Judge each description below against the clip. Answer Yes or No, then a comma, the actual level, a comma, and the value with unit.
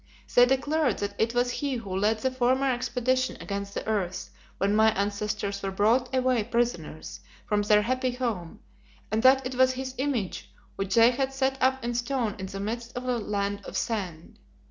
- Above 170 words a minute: Yes, average, 190 wpm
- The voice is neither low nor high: No, high, 235 Hz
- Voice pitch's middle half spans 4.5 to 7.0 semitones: No, average, 4.1 semitones